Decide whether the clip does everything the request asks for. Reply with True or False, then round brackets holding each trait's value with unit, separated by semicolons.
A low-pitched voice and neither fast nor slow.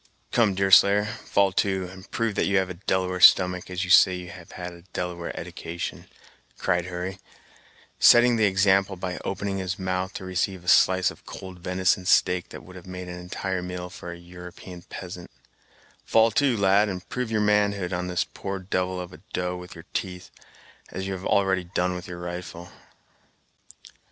True (90 Hz; 180 wpm)